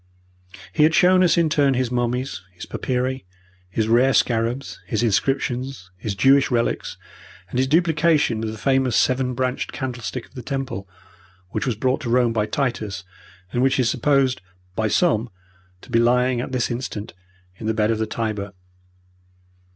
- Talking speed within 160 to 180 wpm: Yes, average, 165 wpm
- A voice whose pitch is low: Yes, low, 125 Hz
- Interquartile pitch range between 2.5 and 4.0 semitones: Yes, average, 3.0 semitones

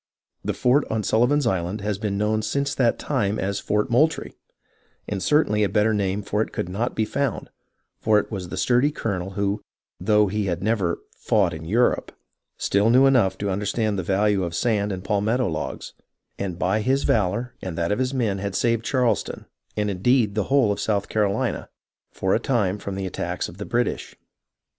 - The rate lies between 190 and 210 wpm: Yes, average, 195 wpm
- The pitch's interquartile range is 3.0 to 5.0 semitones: Yes, average, 3.3 semitones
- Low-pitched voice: Yes, low, 105 Hz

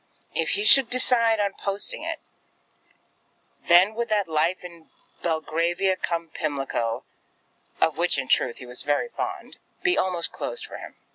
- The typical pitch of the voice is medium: Yes, medium, 180 Hz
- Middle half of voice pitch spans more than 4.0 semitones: Yes, wide, 5.6 semitones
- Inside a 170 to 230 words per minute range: No, average, 150 wpm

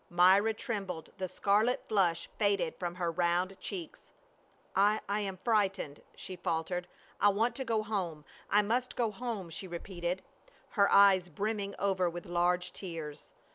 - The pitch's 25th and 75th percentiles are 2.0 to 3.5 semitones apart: Yes, average, 2.9 semitones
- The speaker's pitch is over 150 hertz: Yes, high, 190 Hz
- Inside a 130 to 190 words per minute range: Yes, average, 160 wpm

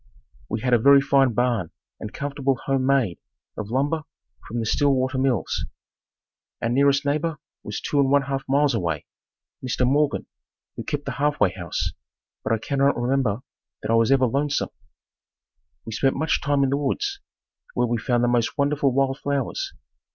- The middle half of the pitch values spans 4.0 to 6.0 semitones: No, average, 2.9 semitones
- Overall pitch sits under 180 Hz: Yes, low, 135 Hz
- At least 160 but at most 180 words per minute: Yes, average, 170 wpm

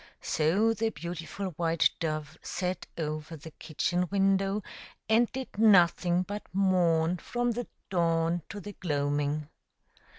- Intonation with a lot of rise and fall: No, average, 3.7 semitones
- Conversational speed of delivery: No, slow, 125 wpm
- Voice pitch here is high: No, medium, 175 Hz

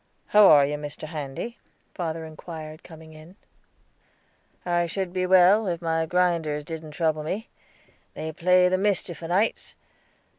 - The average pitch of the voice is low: No, medium, 165 Hz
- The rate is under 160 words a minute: Yes, average, 140 wpm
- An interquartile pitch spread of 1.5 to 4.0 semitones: Yes, average, 2.7 semitones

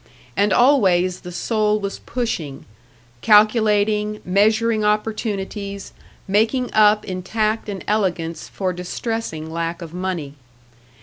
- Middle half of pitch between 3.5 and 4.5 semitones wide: No, average, 3.0 semitones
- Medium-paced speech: No, slow, 110 wpm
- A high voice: Yes, high, 205 Hz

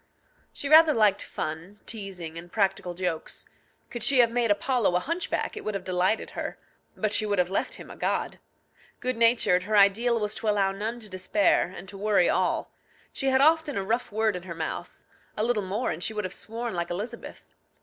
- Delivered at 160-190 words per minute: No, fast, 205 wpm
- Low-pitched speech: No, high, 210 Hz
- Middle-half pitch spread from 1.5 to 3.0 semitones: No, average, 4.0 semitones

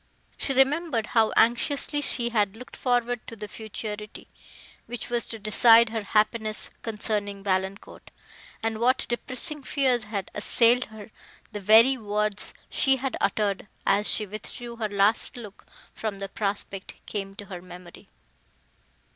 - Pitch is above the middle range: Yes, high, 220 Hz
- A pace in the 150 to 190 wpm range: No, average, 140 wpm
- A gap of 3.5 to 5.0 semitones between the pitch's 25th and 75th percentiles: No, average, 2.7 semitones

